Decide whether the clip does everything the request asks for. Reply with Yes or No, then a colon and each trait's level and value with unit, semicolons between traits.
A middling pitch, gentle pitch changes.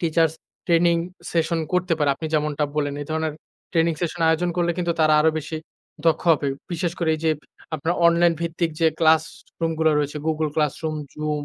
Yes: medium, 160 Hz; narrow, 1.7 semitones